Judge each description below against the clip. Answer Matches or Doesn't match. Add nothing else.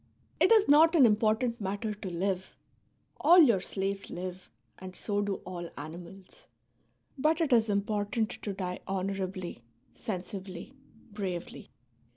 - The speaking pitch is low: Doesn't match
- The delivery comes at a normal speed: Doesn't match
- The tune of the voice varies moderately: Matches